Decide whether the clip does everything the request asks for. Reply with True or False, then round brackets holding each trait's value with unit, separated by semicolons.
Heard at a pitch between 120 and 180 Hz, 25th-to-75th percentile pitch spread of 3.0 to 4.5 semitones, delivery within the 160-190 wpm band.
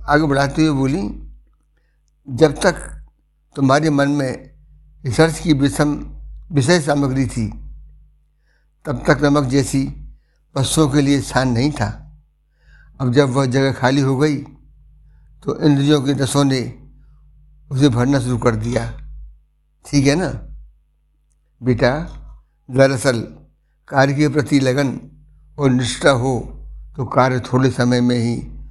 False (135 Hz; 3.9 semitones; 125 wpm)